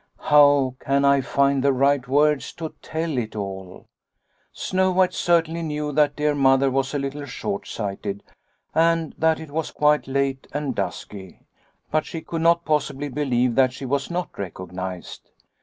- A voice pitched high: No, medium, 140 Hz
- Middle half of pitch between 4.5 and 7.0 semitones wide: No, average, 3.2 semitones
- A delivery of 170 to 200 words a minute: No, average, 160 wpm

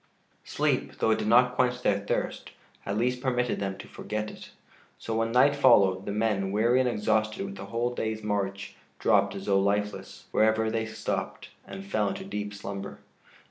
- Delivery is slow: No, average, 185 wpm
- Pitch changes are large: No, average, 3.5 semitones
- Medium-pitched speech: No, low, 110 Hz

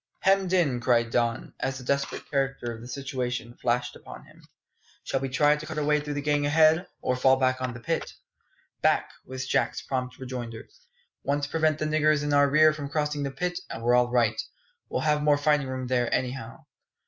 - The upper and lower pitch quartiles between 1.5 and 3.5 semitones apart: Yes, average, 3.1 semitones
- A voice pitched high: No, low, 135 Hz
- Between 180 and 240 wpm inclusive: Yes, fast, 205 wpm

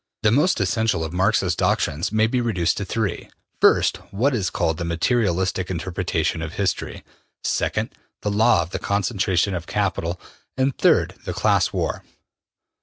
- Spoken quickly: No, average, 160 wpm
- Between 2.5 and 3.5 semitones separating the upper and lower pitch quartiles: No, average, 4.1 semitones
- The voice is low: Yes, very low, 95 Hz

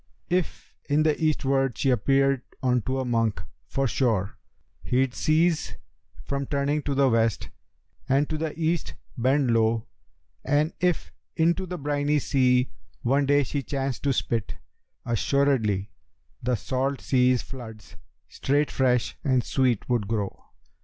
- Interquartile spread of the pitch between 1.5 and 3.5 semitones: Yes, average, 2.9 semitones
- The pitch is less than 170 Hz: Yes, low, 135 Hz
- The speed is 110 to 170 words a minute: Yes, slow, 135 wpm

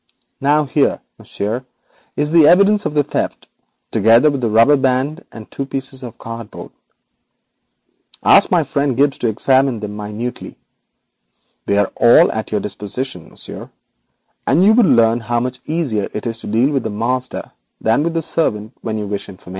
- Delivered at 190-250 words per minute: No, average, 160 wpm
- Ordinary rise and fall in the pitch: Yes, average, 4.5 semitones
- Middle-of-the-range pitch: No, low, 125 Hz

